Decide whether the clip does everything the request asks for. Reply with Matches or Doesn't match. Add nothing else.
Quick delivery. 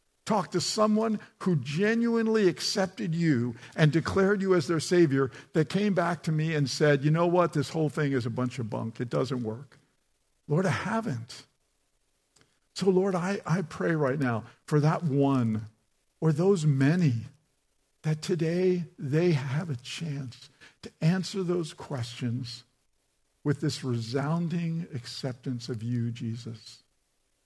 Doesn't match